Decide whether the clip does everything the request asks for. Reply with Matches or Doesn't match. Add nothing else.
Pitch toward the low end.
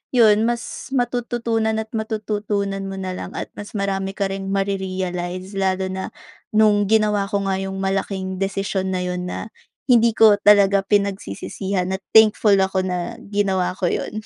Doesn't match